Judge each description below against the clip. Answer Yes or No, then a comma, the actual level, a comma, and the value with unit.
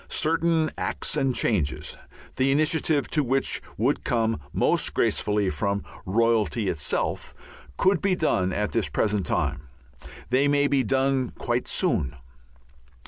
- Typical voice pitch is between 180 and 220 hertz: No, low, 120 Hz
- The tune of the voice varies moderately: No, wide, 5.9 semitones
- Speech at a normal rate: No, slow, 130 wpm